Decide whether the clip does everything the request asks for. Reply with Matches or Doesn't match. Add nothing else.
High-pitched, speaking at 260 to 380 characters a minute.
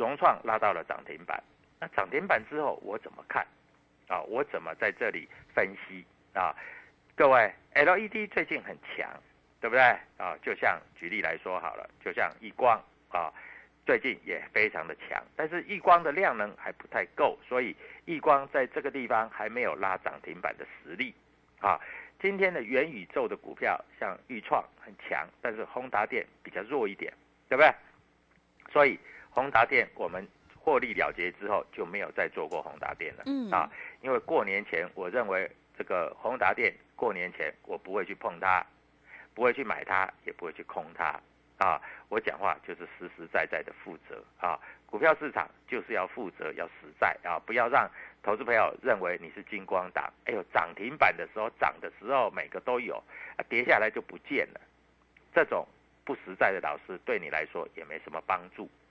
Matches